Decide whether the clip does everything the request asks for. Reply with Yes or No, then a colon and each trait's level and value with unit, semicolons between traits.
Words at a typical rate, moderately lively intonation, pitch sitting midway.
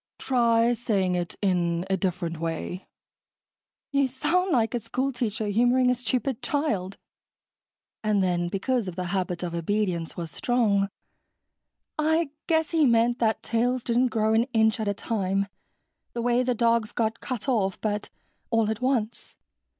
No: average, 155 wpm; average, 4.4 semitones; high, 225 Hz